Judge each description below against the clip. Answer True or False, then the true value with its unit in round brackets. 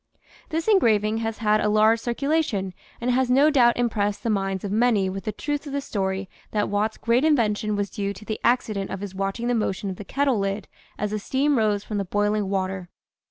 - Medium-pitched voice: False (215 Hz)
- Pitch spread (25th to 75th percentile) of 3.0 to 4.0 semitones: True (3.5 semitones)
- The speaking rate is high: True (215 wpm)